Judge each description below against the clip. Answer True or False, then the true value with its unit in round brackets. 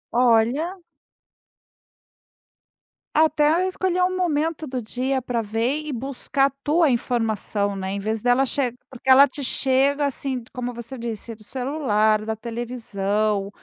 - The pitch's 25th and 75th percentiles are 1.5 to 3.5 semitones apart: False (4.2 semitones)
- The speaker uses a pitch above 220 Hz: True (250 Hz)